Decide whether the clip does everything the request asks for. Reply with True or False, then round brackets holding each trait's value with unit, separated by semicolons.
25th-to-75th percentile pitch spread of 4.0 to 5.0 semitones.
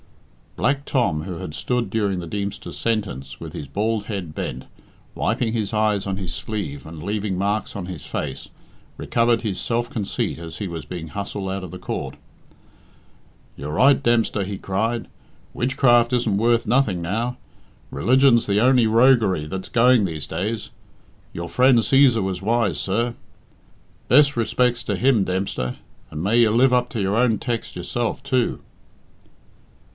True (4.3 semitones)